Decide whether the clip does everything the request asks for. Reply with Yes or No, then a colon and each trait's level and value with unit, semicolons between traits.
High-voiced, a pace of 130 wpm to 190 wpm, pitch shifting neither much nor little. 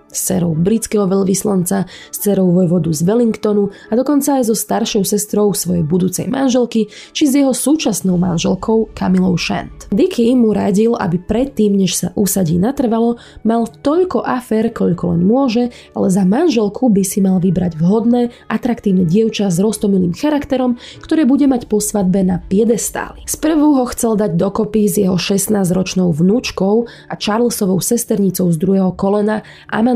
Yes: high, 210 Hz; average, 150 wpm; average, 4.0 semitones